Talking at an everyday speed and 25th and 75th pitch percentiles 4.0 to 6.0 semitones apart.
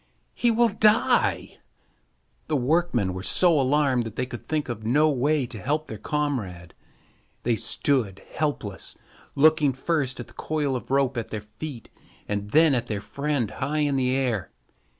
Yes: average, 165 wpm; average, 4.7 semitones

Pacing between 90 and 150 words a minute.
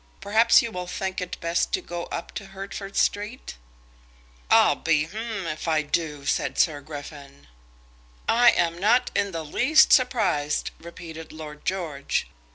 Yes: average, 145 wpm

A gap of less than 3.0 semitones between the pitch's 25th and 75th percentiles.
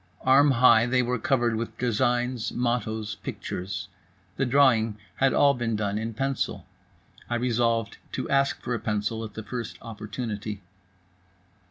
Yes: narrow, 2.4 semitones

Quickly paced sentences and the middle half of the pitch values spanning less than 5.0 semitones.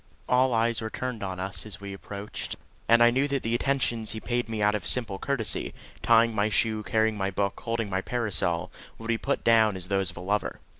Yes: fast, 220 wpm; average, 2.9 semitones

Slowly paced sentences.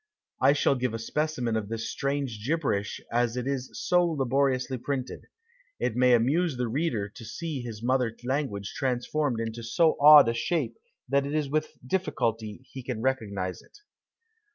No: average, 165 wpm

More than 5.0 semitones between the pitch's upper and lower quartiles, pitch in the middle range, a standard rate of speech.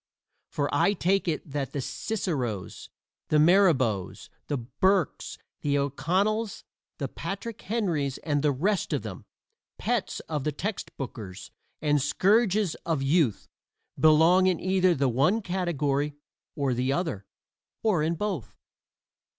No: wide, 5.5 semitones; medium, 155 Hz; slow, 130 wpm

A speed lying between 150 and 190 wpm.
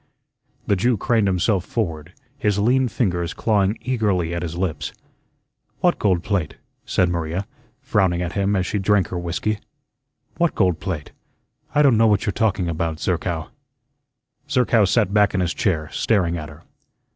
Yes: average, 160 wpm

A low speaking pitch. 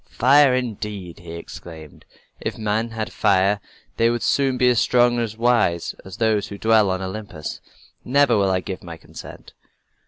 Yes: low, 110 Hz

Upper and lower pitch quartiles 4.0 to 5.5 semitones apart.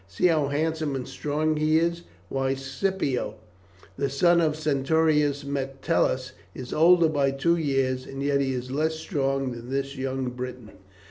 No: average, 2.9 semitones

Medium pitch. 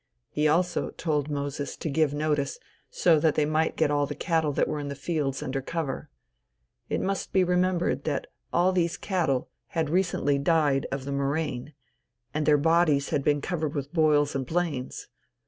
Yes: medium, 150 Hz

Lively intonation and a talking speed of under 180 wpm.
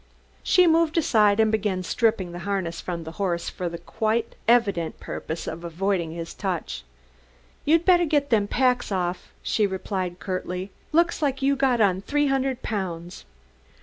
Yes: wide, 6.8 semitones; average, 160 wpm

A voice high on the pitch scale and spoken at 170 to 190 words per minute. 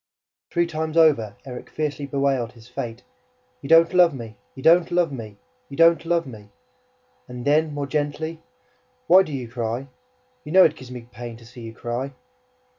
No: medium, 140 Hz; average, 180 wpm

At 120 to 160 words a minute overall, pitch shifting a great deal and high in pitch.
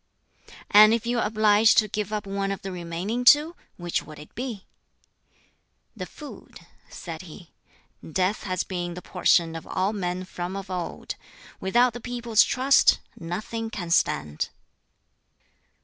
No: average, 150 wpm; average, 4.2 semitones; high, 195 Hz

